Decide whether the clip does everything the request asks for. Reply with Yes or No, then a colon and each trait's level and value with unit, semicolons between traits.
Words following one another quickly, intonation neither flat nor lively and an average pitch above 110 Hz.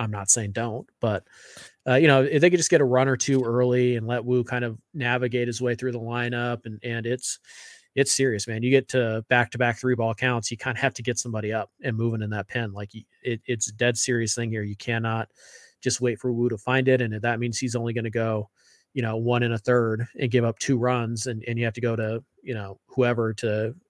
No: fast, 265 wpm; narrow, 1.7 semitones; low, 120 Hz